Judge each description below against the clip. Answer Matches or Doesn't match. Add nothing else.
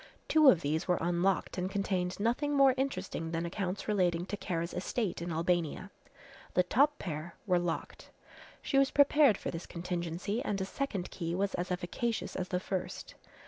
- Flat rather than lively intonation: Doesn't match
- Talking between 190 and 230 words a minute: Doesn't match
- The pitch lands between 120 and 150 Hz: Doesn't match